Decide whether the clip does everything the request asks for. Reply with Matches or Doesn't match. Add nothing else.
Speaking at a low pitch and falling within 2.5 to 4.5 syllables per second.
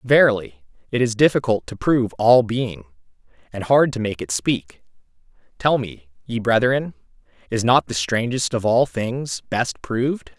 Matches